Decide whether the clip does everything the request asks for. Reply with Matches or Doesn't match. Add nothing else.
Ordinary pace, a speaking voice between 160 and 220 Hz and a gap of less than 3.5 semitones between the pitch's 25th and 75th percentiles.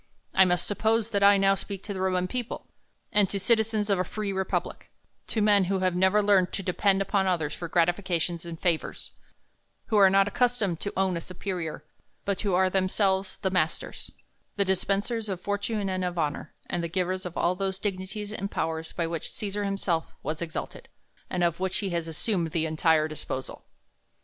Matches